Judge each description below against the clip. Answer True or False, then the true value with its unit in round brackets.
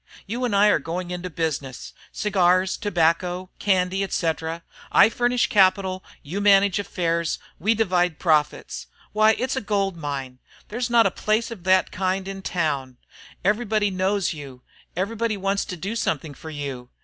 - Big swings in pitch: False (3.8 semitones)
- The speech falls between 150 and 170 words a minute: True (155 wpm)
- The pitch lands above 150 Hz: True (185 Hz)